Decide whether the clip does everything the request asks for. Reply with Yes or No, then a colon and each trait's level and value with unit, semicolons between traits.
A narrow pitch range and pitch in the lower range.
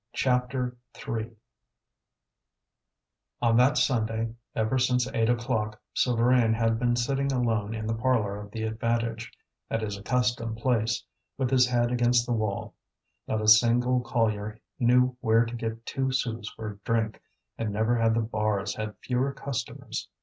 Yes: narrow, 2.0 semitones; low, 115 Hz